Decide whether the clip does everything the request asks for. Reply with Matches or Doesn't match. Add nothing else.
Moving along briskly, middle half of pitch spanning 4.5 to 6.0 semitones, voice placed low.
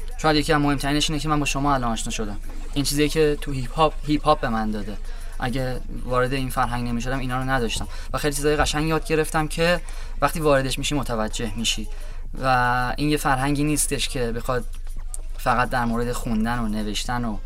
Matches